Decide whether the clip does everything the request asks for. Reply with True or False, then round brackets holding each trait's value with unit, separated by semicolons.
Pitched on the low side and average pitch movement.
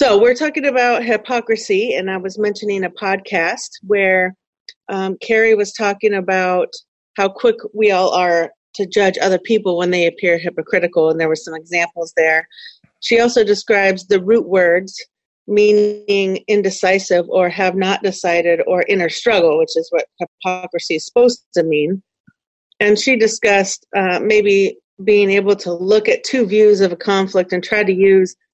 False (195 Hz; 3.3 semitones)